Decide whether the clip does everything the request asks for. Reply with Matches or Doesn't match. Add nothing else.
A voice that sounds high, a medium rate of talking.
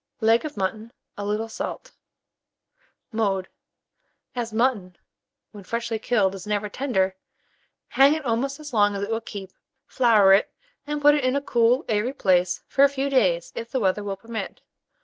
Matches